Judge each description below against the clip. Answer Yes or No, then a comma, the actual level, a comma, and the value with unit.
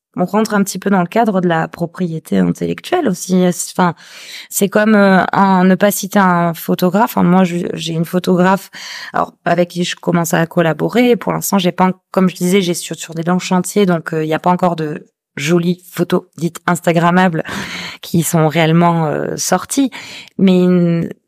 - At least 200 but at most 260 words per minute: No, average, 190 wpm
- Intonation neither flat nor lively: No, narrow, 1.9 semitones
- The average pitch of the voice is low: No, medium, 180 Hz